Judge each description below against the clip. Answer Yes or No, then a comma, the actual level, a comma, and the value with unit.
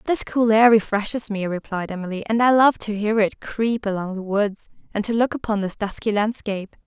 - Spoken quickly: Yes, fast, 210 wpm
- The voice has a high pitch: Yes, high, 210 Hz